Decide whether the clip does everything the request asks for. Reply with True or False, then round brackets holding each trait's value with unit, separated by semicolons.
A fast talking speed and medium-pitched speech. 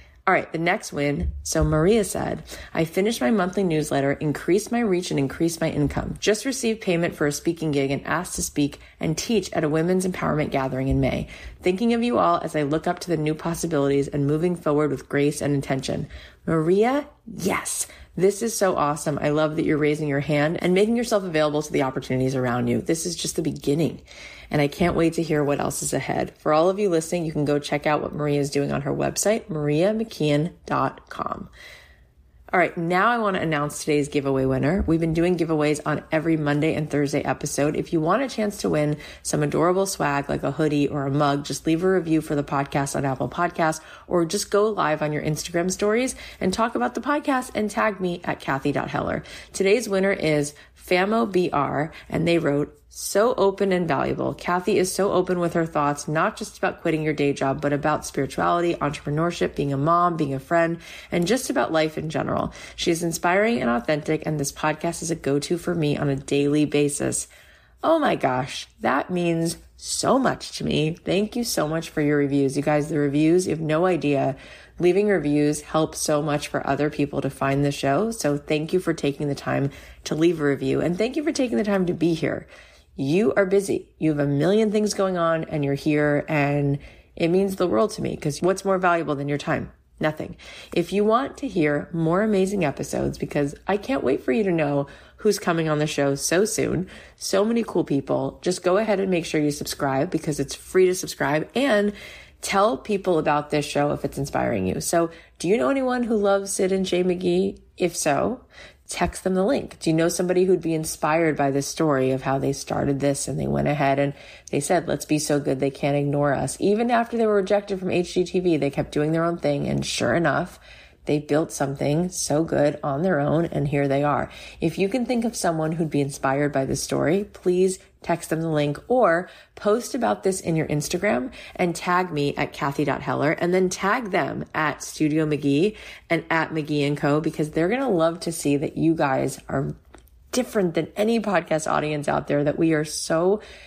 True (215 wpm; 160 Hz)